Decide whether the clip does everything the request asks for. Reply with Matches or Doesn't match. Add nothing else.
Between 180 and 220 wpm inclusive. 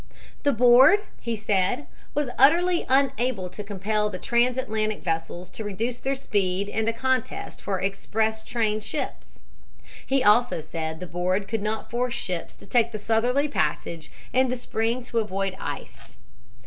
Doesn't match